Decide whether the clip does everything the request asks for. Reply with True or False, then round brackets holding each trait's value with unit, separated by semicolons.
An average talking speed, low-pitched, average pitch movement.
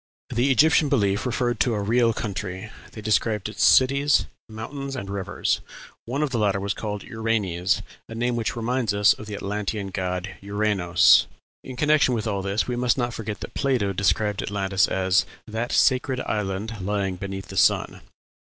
True (170 wpm; 105 Hz; 3.6 semitones)